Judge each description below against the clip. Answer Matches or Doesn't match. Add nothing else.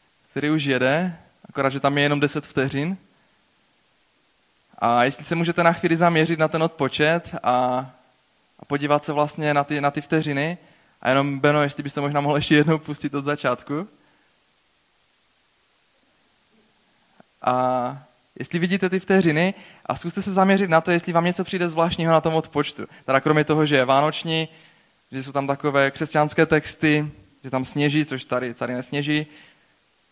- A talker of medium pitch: Matches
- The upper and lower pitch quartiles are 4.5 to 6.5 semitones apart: Doesn't match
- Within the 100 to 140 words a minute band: Doesn't match